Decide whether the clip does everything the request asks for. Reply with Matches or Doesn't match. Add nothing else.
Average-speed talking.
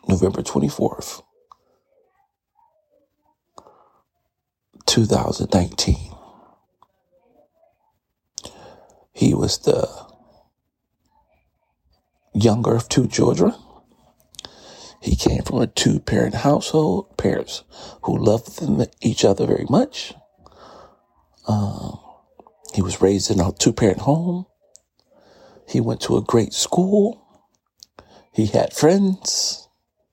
Doesn't match